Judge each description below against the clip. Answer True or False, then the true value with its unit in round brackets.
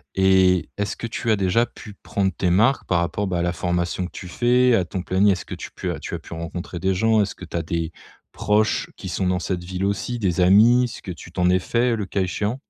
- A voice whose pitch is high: False (95 Hz)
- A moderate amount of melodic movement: True (3.2 semitones)